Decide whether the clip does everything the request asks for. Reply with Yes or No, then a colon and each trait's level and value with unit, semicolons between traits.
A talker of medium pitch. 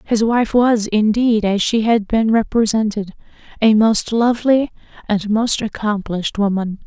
No: high, 220 Hz